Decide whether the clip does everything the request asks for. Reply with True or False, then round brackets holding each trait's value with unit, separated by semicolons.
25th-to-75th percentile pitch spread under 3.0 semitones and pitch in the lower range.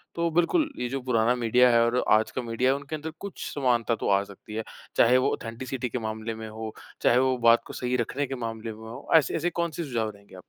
False (3.3 semitones; 125 Hz)